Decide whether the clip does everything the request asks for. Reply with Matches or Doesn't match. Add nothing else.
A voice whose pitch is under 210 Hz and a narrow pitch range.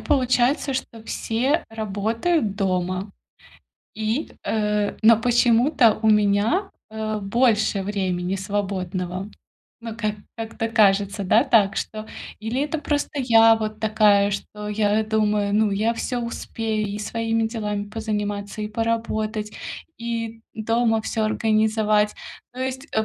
Doesn't match